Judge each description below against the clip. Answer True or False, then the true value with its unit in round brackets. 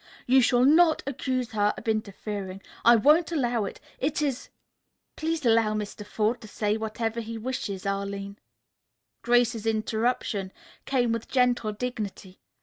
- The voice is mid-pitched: False (225 Hz)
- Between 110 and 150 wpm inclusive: True (145 wpm)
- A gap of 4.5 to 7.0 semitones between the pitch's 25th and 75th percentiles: False (3.1 semitones)